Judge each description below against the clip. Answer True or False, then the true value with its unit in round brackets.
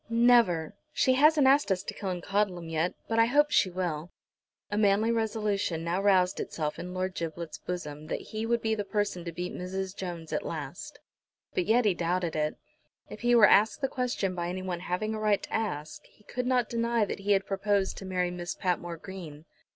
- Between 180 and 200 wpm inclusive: True (195 wpm)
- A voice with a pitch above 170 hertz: True (190 Hz)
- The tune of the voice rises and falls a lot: False (3.9 semitones)